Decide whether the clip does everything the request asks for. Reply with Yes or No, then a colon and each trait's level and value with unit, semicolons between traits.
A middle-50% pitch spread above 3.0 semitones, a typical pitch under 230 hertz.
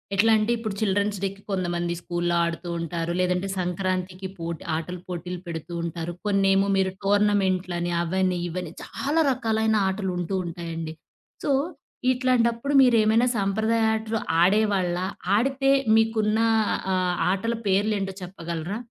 Yes: average, 3.8 semitones; high, 190 Hz